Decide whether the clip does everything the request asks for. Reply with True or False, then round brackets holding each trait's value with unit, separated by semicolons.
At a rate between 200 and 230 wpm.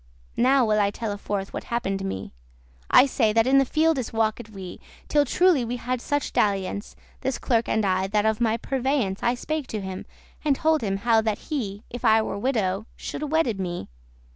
True (205 wpm)